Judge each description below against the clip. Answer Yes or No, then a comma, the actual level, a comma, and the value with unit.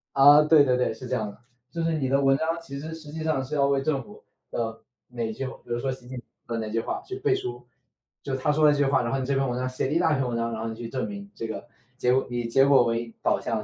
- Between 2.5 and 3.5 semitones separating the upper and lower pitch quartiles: No, average, 3.9 semitones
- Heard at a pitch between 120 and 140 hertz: Yes, low, 135 Hz